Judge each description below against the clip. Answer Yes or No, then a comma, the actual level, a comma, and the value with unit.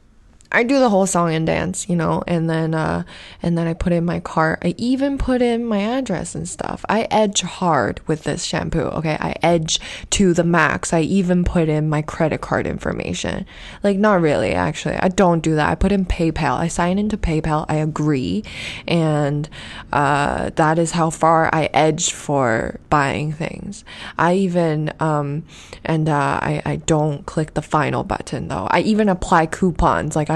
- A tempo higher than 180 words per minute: Yes, average, 190 wpm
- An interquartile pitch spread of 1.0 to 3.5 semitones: Yes, average, 3.2 semitones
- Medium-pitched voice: Yes, medium, 165 Hz